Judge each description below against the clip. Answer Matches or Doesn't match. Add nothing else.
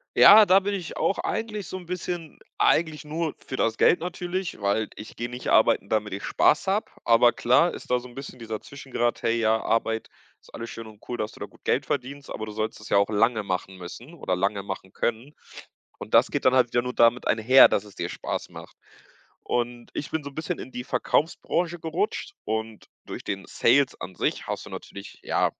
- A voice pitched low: Matches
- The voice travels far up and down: Matches